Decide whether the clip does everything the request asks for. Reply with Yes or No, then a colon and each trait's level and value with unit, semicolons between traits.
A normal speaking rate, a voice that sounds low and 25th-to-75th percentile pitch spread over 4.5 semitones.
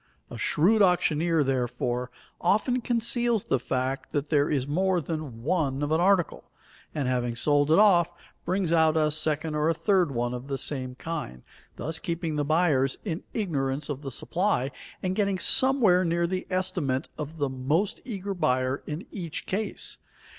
No: average, 170 wpm; medium, 155 Hz; average, 5.2 semitones